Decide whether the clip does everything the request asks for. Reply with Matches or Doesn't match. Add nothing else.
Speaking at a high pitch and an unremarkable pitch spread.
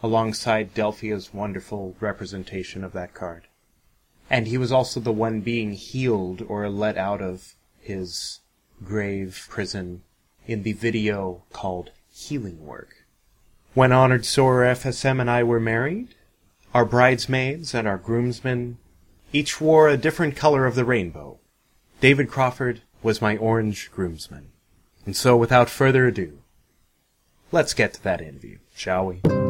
Doesn't match